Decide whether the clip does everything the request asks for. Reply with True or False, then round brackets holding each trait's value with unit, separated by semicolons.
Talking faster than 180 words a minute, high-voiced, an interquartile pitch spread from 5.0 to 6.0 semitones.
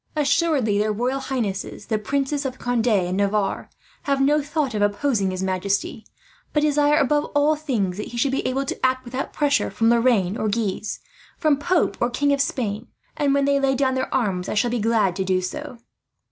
True (200 wpm; 250 Hz; 5.3 semitones)